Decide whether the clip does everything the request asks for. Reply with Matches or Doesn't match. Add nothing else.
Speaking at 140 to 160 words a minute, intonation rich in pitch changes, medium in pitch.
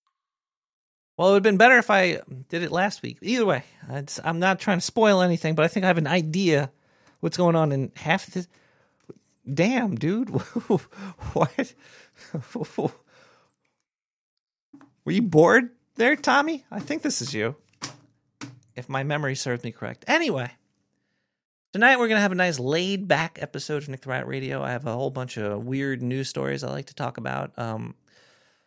Doesn't match